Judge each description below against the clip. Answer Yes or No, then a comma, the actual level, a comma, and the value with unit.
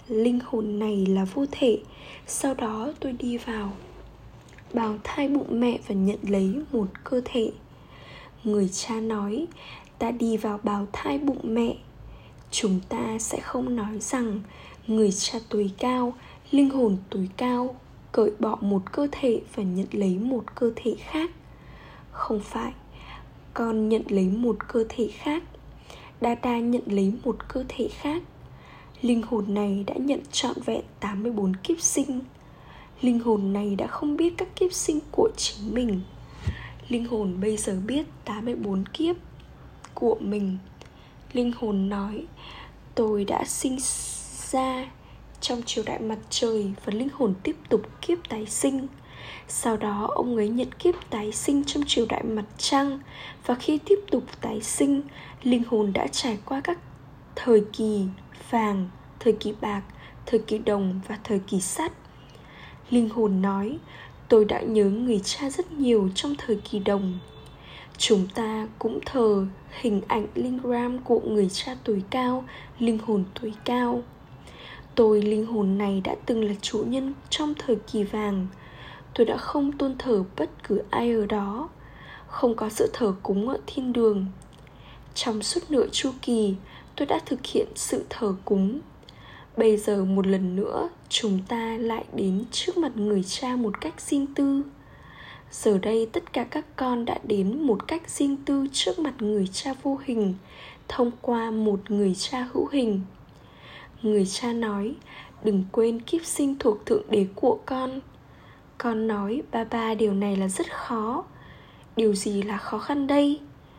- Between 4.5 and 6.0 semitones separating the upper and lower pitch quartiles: No, average, 3.8 semitones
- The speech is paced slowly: Yes, slow, 160 wpm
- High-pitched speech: Yes, high, 225 Hz